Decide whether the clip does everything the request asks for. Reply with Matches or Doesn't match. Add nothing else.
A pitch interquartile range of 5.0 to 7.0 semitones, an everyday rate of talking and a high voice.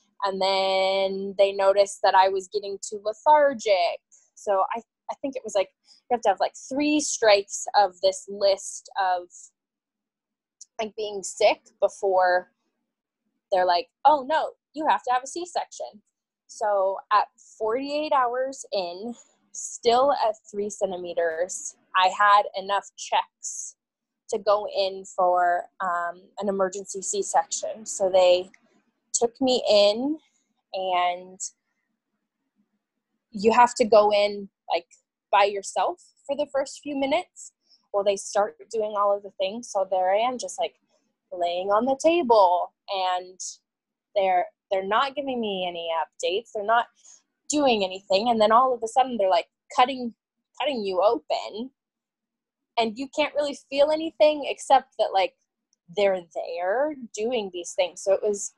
Matches